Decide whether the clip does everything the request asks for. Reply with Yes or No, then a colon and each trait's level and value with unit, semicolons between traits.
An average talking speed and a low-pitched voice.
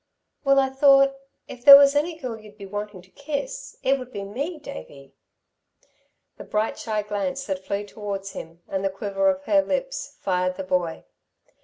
No: average, 180 wpm; high, 215 Hz